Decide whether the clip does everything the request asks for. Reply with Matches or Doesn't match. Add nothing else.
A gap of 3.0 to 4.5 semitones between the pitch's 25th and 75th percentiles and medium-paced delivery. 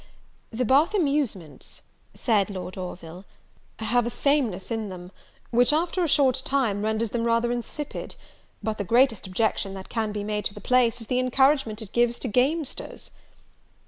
Matches